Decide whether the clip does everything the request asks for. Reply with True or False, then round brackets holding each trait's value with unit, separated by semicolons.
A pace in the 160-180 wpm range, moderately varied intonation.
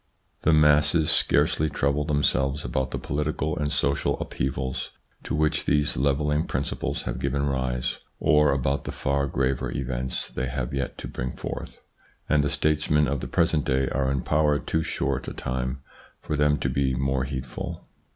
False (170 wpm; 2.1 semitones)